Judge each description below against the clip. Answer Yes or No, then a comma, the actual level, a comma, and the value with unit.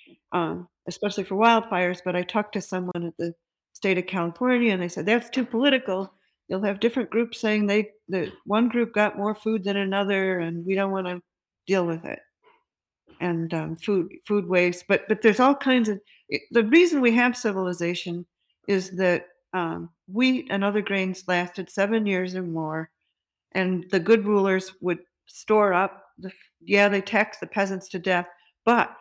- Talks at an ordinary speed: Yes, average, 180 wpm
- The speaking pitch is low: No, high, 195 Hz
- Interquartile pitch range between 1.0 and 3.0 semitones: No, average, 3.4 semitones